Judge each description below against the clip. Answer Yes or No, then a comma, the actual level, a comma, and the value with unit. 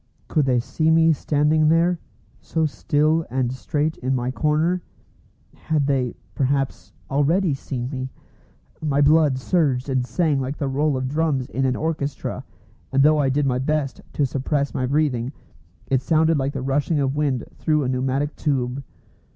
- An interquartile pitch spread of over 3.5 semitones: No, average, 2.7 semitones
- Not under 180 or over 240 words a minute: No, average, 165 wpm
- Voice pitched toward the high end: No, medium, 140 Hz